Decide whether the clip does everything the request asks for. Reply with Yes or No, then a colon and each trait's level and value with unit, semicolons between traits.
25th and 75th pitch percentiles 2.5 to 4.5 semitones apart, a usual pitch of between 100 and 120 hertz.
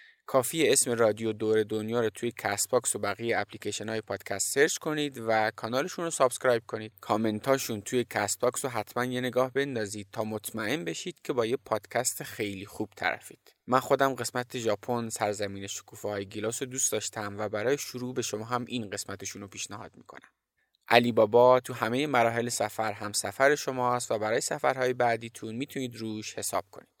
Yes: average, 2.9 semitones; low, 115 Hz